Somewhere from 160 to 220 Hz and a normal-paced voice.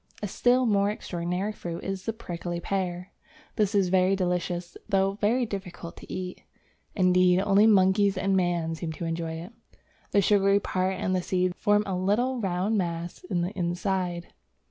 Yes: medium, 185 Hz; average, 170 wpm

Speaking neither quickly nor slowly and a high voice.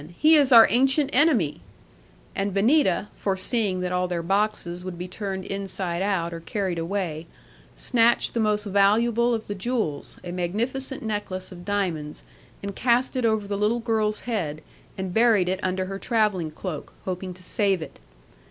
Yes: average, 165 wpm; high, 200 Hz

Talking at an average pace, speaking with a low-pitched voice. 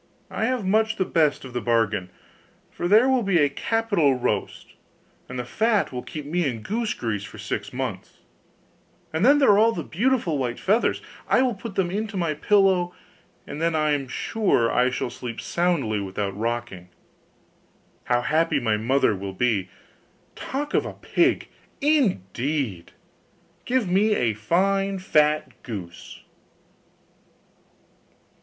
No: average, 150 wpm; medium, 155 Hz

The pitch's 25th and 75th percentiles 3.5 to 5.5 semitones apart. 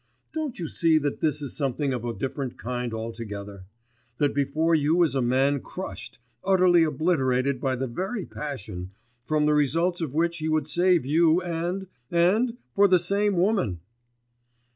Yes: average, 5.0 semitones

